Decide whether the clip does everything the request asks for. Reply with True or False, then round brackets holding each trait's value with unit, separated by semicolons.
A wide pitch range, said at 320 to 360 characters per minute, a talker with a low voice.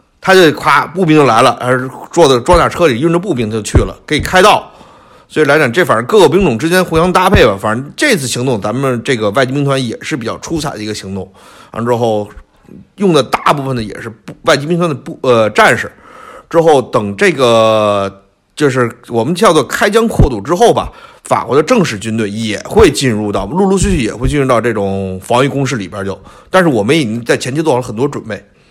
True (6.1 semitones; 325 characters per minute; 125 Hz)